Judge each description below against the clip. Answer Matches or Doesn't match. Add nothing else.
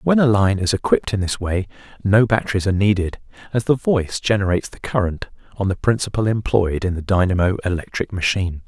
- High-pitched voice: Doesn't match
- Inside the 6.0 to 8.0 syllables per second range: Matches